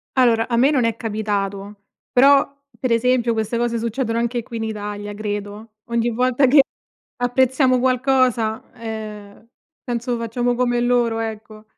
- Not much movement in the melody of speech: Yes, narrow, 2.3 semitones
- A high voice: Yes, high, 235 Hz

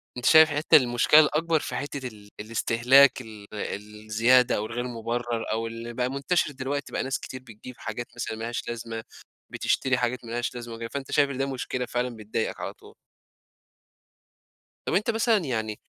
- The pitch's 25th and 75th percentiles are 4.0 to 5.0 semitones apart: No, average, 3.1 semitones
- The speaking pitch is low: Yes, low, 120 Hz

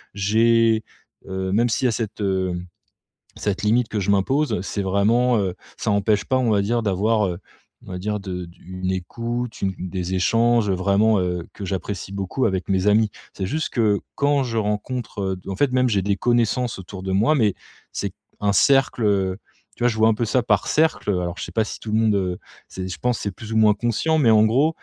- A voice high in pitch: No, low, 105 Hz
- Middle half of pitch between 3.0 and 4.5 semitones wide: Yes, average, 3.5 semitones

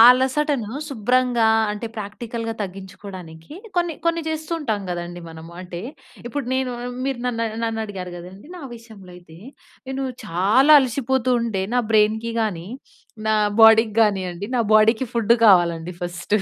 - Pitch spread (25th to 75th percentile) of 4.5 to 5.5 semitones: Yes, average, 5.2 semitones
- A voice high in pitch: Yes, high, 220 Hz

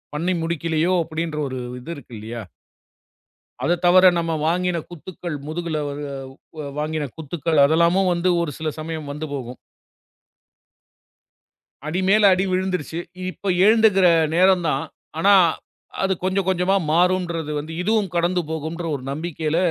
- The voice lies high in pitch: No, medium, 170 Hz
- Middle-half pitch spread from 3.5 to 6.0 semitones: No, average, 2.8 semitones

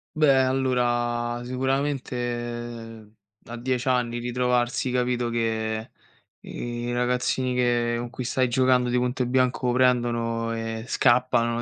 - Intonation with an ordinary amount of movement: No, narrow, 1.1 semitones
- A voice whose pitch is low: Yes, low, 120 Hz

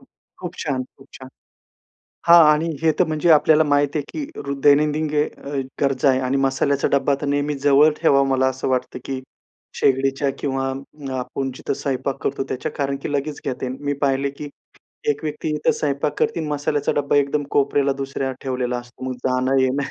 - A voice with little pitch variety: Yes, narrow, 1.8 semitones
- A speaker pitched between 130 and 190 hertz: Yes, medium, 140 Hz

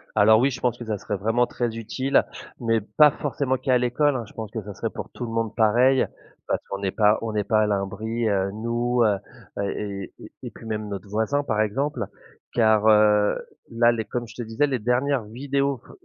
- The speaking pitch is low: Yes, low, 115 Hz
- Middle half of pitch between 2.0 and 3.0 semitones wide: Yes, average, 2.7 semitones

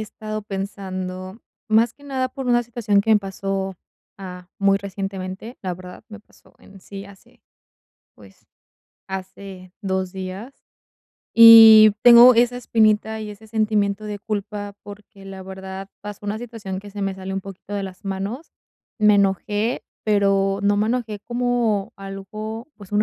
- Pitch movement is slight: Yes, narrow, 2.2 semitones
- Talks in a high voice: Yes, high, 205 Hz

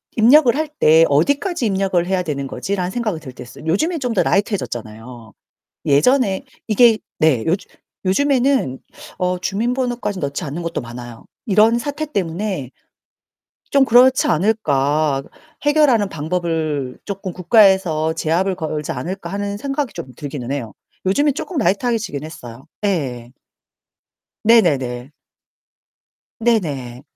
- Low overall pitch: No, medium, 185 Hz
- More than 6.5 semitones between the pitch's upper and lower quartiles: Yes, wide, 8.0 semitones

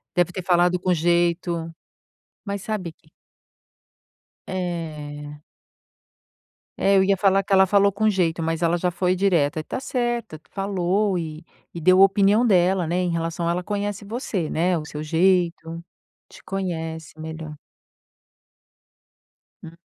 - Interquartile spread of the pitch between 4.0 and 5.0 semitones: No, average, 2.9 semitones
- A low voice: No, medium, 175 Hz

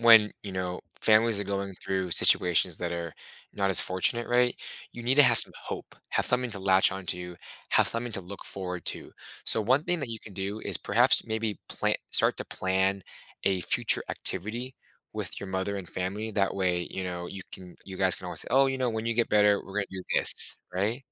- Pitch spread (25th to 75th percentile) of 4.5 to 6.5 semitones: No, average, 3.4 semitones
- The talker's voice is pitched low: Yes, low, 100 Hz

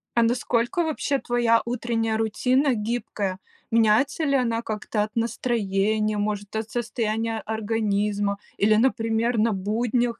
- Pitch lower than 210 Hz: No, high, 225 Hz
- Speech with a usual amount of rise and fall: No, narrow, 2.1 semitones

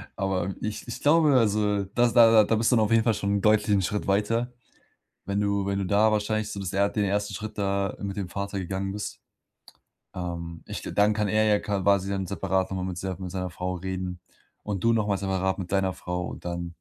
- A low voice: Yes, low, 100 Hz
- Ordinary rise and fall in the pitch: No, narrow, 2.0 semitones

